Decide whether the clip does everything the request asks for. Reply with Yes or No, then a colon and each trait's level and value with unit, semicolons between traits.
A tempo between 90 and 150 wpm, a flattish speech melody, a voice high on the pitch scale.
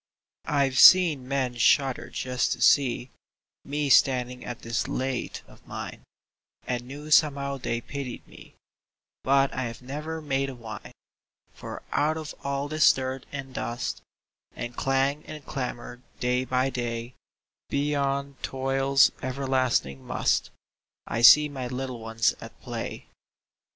No: slow, 135 wpm; narrow, 2.0 semitones; low, 135 Hz